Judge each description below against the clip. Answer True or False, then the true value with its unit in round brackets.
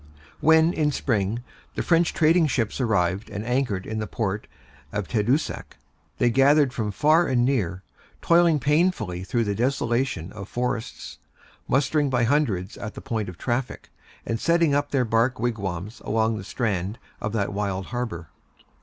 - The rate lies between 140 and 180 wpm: True (155 wpm)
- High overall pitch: False (120 Hz)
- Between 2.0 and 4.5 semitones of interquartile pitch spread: False (5.3 semitones)